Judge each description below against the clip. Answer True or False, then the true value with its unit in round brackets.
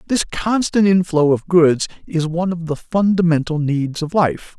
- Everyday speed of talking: True (170 wpm)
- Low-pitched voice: False (170 Hz)